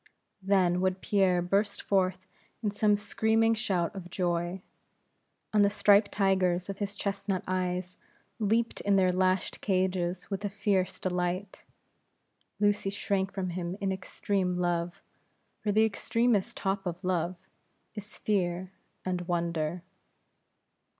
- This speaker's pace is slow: Yes, slow, 130 wpm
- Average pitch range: No, narrow, 2.0 semitones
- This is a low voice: No, high, 190 Hz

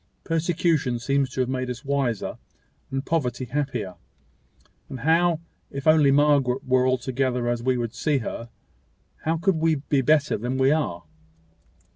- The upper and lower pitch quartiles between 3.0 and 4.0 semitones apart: Yes, average, 3.4 semitones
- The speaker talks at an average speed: Yes, average, 150 wpm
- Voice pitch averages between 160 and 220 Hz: No, low, 135 Hz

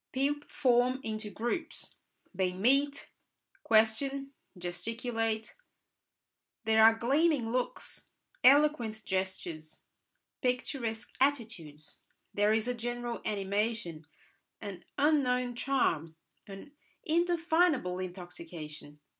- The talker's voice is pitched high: Yes, high, 225 Hz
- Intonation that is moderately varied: No, wide, 6.0 semitones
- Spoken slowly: Yes, slow, 85 wpm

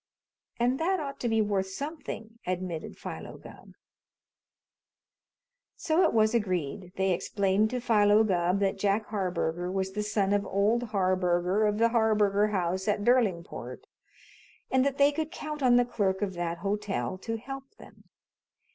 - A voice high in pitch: Yes, high, 205 Hz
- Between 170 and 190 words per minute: No, average, 155 wpm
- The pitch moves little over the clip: No, average, 3.7 semitones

